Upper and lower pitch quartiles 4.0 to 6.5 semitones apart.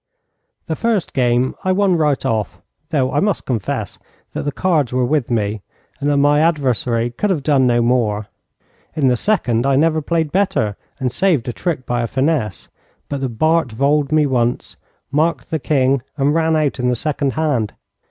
Yes: average, 4.4 semitones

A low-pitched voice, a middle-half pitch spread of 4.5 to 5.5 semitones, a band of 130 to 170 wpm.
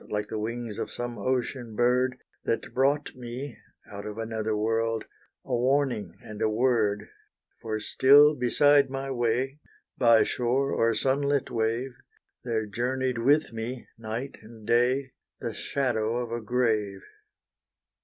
No: low, 120 Hz; average, 2.8 semitones; slow, 135 wpm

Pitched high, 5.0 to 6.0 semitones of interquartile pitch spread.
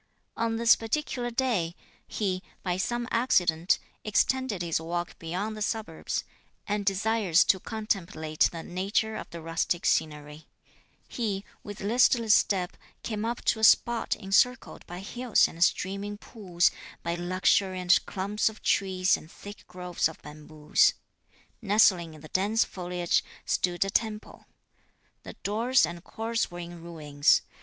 No: high, 195 Hz; average, 4.3 semitones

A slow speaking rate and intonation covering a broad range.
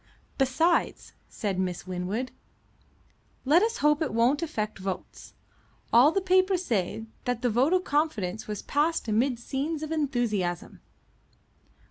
Yes: slow, 130 wpm; wide, 6.8 semitones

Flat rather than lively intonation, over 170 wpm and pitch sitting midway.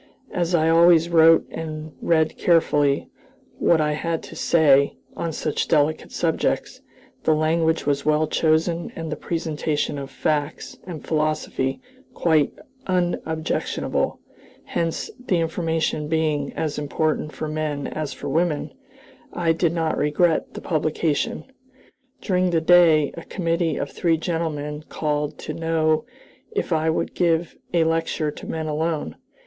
No: narrow, 1.6 semitones; slow, 135 wpm; medium, 160 Hz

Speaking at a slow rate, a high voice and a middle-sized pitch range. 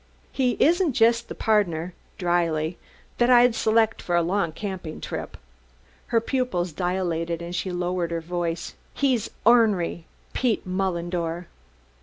No: slow, 130 wpm; medium, 180 Hz; average, 4.9 semitones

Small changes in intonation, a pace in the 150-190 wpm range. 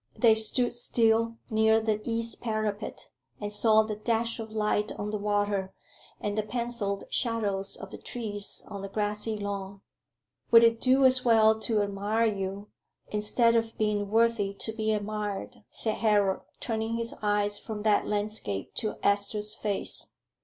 Yes: narrow, 1.7 semitones; average, 155 wpm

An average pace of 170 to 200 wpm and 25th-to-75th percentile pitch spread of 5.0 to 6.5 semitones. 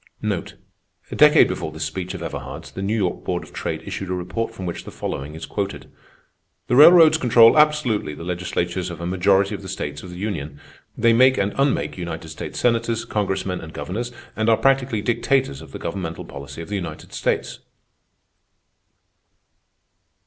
Yes: average, 175 wpm; average, 5.3 semitones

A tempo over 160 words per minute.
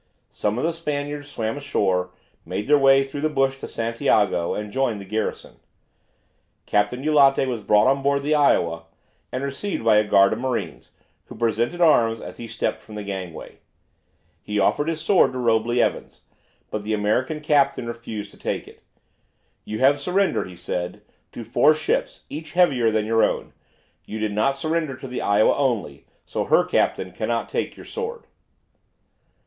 Yes: average, 175 wpm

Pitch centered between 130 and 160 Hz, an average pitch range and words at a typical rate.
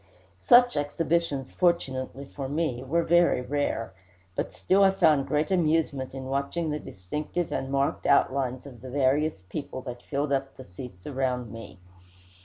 Yes: medium, 140 Hz; average, 3.3 semitones; average, 155 wpm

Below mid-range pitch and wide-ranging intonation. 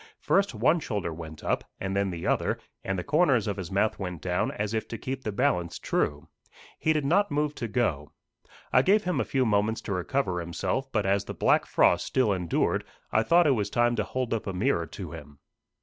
Yes: low, 105 Hz; wide, 6.7 semitones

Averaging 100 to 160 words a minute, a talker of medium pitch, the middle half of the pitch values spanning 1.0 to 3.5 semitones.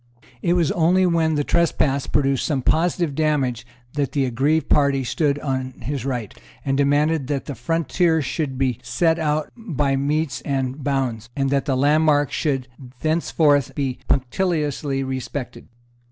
Yes: average, 150 wpm; medium, 145 Hz; average, 2.8 semitones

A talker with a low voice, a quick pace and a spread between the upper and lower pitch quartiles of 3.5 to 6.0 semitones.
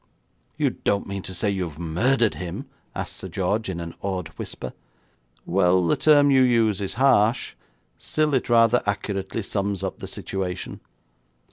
No: low, 100 Hz; average, 155 wpm; average, 4.1 semitones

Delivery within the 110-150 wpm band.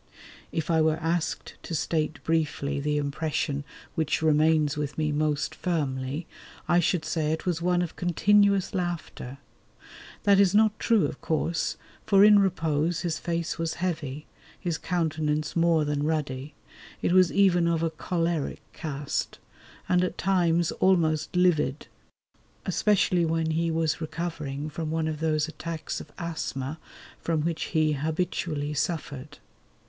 Yes: average, 145 wpm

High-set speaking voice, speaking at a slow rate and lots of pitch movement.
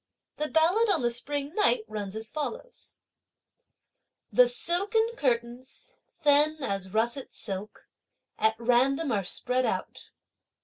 Yes: very high, 275 Hz; slow, 120 wpm; wide, 6.7 semitones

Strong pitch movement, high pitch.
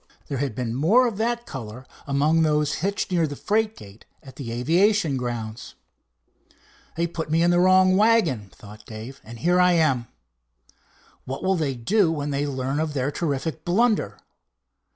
No: wide, 6.0 semitones; medium, 150 Hz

